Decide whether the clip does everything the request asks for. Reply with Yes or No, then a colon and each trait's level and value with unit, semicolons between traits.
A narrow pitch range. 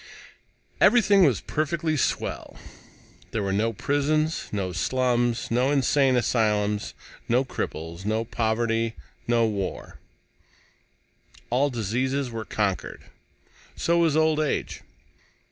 No: average, 4.7 semitones